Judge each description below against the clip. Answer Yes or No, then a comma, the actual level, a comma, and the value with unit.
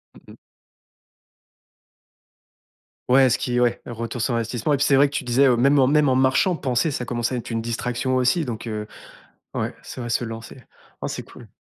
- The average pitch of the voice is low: Yes, low, 125 Hz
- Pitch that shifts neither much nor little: No, narrow, 2.2 semitones